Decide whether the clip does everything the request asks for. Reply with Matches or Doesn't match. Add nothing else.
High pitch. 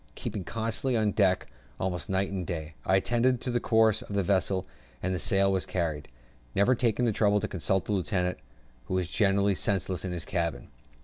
Doesn't match